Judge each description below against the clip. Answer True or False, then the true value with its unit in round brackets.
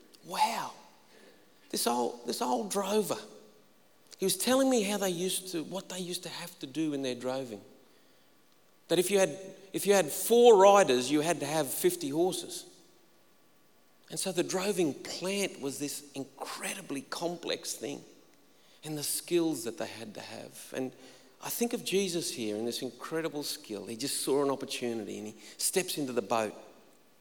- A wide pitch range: True (6.5 semitones)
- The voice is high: False (165 Hz)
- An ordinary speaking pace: True (170 wpm)